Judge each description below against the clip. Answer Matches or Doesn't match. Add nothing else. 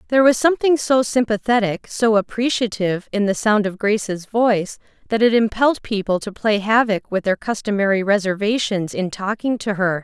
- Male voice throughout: Doesn't match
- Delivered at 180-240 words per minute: Doesn't match